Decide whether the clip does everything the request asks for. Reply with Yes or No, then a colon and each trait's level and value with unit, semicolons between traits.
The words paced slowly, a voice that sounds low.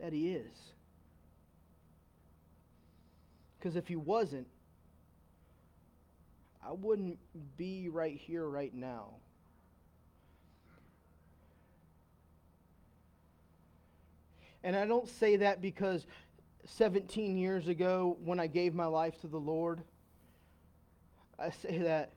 Yes: slow, 90 wpm; very low, 85 Hz